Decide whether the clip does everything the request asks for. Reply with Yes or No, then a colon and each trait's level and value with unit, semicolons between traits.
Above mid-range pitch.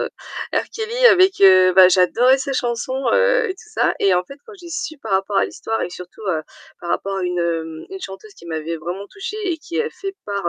Yes: high, 205 Hz